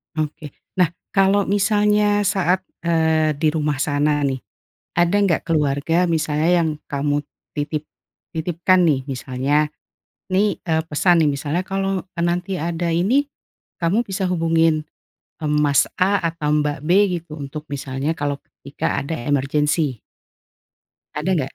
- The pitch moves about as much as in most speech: Yes, average, 3.6 semitones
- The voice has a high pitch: No, medium, 160 Hz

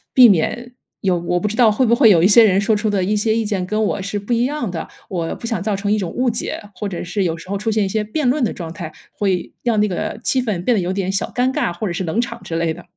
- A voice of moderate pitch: No, high, 205 Hz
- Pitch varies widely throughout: No, average, 4.0 semitones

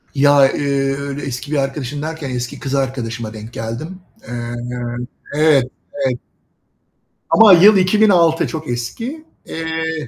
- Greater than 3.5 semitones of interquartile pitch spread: Yes, average, 4.2 semitones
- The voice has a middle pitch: Yes, medium, 145 Hz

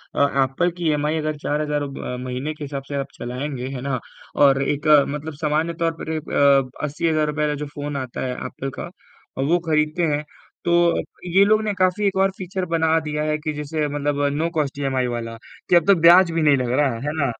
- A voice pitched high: No, medium, 150 Hz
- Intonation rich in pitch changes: No, average, 2.9 semitones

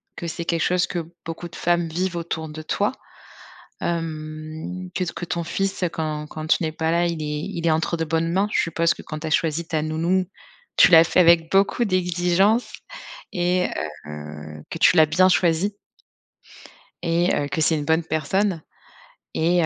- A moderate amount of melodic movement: No, narrow, 2.1 semitones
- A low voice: No, medium, 165 Hz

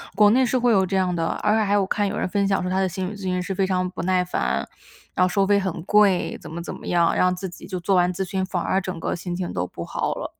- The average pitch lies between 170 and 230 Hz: Yes, medium, 185 Hz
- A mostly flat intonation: Yes, narrow, 1.7 semitones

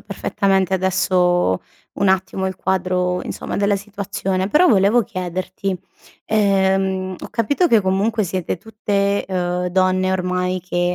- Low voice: No, high, 190 Hz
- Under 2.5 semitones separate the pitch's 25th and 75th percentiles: Yes, narrow, 1.5 semitones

